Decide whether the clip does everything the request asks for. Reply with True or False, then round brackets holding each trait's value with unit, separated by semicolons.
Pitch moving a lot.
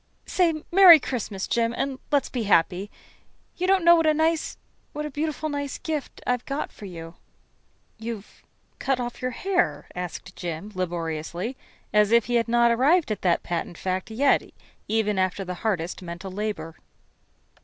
True (7.7 semitones)